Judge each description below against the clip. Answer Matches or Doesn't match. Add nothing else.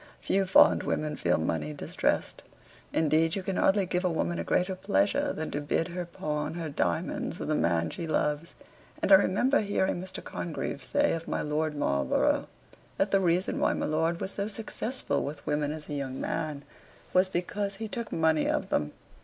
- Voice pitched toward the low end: Doesn't match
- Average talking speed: Matches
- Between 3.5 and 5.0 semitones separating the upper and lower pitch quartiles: Matches